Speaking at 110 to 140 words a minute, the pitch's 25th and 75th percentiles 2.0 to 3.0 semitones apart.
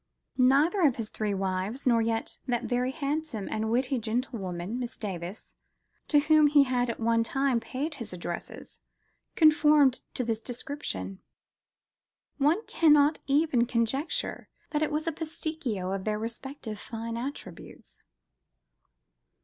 No: slow, 135 wpm; average, 4.9 semitones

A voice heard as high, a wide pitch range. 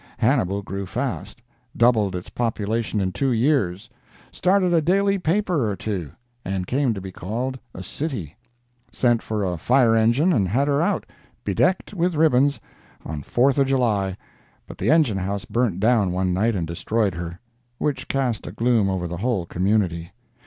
No: low, 115 Hz; wide, 5.9 semitones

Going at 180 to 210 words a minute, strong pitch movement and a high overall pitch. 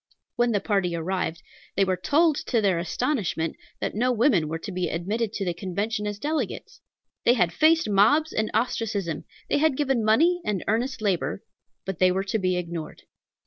No: average, 185 wpm; average, 5.0 semitones; high, 205 Hz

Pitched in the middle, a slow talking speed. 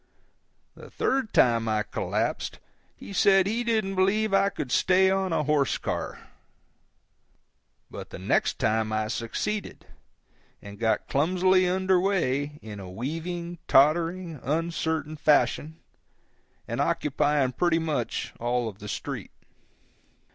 Yes: medium, 160 Hz; slow, 125 wpm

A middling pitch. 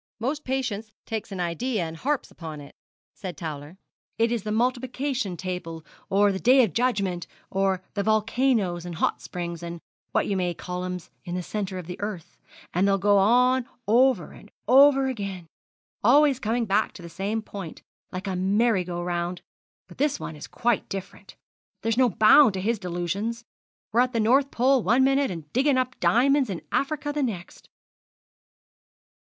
No: high, 210 Hz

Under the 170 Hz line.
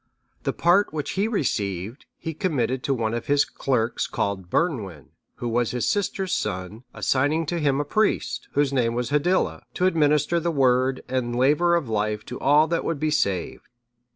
Yes: low, 135 Hz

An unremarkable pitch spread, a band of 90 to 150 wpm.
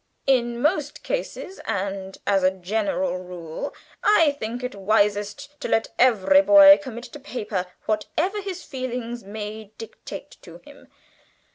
No: wide, 6.1 semitones; slow, 135 wpm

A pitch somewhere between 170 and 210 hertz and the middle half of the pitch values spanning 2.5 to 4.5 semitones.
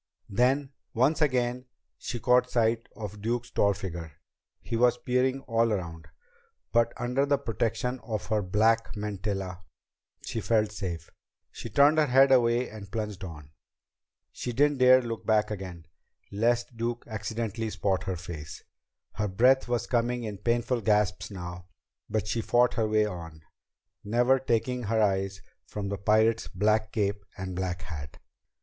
No: low, 110 Hz; average, 3.6 semitones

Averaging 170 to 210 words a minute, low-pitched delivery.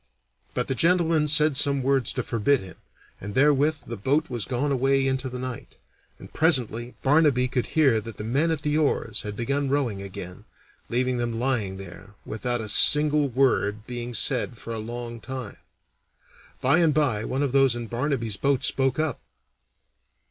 Yes: average, 175 wpm; low, 130 Hz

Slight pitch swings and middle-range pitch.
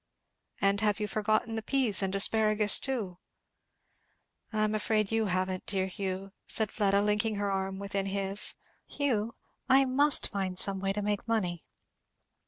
No: narrow, 2.1 semitones; high, 205 Hz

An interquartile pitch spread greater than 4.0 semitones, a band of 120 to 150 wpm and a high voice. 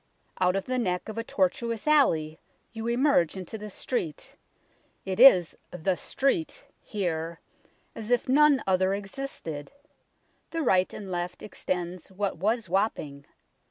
Yes: average, 4.9 semitones; average, 145 wpm; high, 195 Hz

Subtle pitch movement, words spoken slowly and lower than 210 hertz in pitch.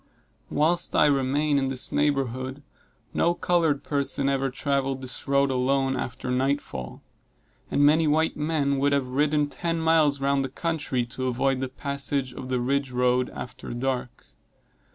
No: narrow, 2.1 semitones; average, 155 wpm; medium, 140 Hz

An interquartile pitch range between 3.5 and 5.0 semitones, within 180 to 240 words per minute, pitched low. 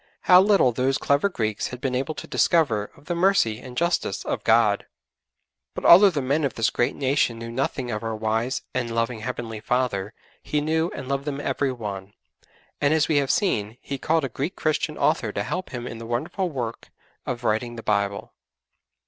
Yes: average, 4.6 semitones; average, 200 wpm; low, 130 Hz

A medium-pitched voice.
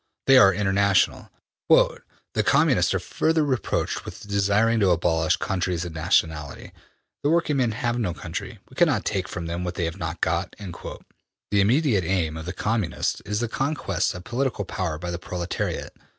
No: very low, 95 Hz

